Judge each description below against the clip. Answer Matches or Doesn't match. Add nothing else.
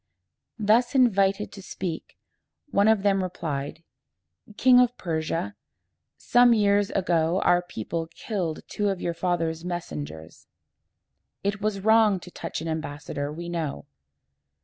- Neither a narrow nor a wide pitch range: Matches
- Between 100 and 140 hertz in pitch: Doesn't match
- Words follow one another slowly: Matches